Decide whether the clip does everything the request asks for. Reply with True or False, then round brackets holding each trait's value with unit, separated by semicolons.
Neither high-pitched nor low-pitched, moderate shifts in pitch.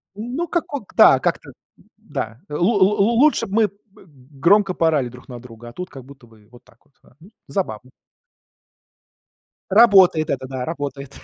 False (155 Hz; 8.2 semitones)